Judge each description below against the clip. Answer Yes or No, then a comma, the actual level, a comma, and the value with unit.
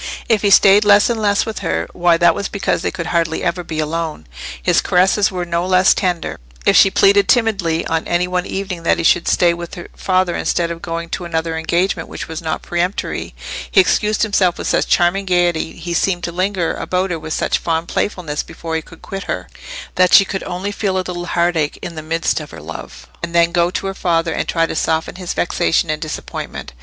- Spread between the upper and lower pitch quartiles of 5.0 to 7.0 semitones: No, narrow, 2.4 semitones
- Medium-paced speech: No, fast, 220 wpm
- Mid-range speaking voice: Yes, medium, 175 Hz